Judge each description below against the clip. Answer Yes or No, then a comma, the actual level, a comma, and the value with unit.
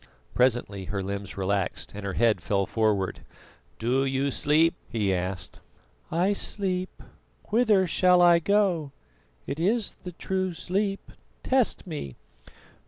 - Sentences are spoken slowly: Yes, slow, 125 wpm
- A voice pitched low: No, medium, 145 Hz